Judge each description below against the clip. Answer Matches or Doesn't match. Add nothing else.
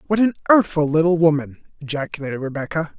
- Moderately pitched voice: Matches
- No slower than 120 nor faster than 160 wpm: Matches